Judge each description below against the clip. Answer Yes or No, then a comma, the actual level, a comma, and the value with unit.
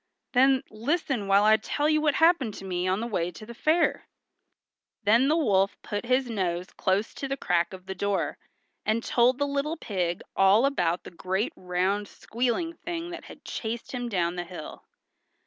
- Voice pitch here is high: Yes, high, 215 Hz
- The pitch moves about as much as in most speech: No, wide, 6.3 semitones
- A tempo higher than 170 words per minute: Yes, average, 185 wpm